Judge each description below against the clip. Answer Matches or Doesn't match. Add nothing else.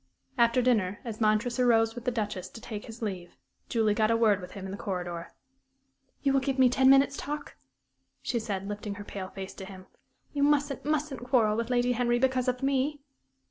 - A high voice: Matches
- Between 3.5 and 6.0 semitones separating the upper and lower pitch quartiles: Matches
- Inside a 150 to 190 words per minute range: Doesn't match